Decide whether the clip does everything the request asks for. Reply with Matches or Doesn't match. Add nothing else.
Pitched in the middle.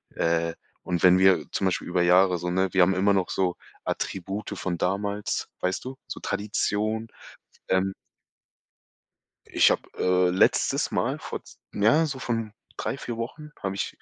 Doesn't match